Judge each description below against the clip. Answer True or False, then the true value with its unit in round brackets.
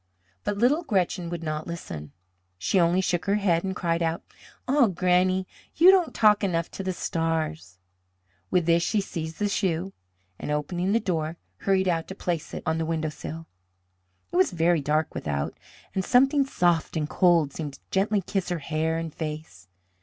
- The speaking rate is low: False (175 wpm)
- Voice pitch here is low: False (170 Hz)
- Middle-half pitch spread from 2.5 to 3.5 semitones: True (3.1 semitones)